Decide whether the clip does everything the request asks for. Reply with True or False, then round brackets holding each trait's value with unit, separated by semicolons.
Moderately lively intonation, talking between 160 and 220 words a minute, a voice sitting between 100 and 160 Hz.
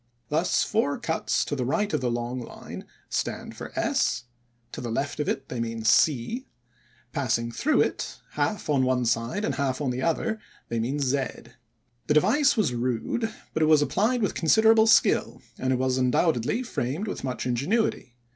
False (8.7 semitones; 180 wpm; 140 Hz)